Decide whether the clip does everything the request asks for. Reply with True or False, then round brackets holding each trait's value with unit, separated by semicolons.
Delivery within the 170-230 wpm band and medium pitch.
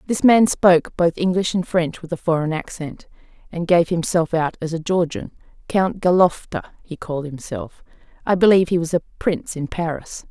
True (175 wpm; 170 Hz)